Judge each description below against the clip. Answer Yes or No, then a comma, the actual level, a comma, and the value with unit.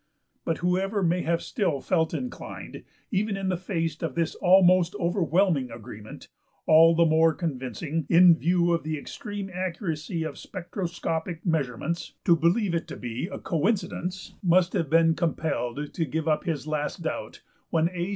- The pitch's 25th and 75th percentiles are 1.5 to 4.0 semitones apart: Yes, narrow, 2.6 semitones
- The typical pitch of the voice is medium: Yes, medium, 170 Hz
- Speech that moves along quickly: No, average, 160 wpm